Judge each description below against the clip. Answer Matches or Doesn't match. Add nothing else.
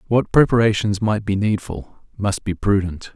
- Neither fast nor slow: Matches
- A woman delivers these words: Doesn't match